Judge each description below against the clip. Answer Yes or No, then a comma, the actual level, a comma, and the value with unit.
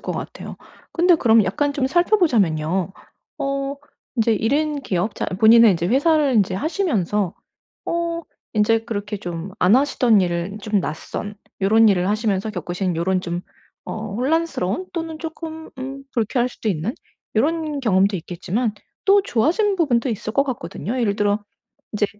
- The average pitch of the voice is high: Yes, high, 225 Hz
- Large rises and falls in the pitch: Yes, wide, 6.7 semitones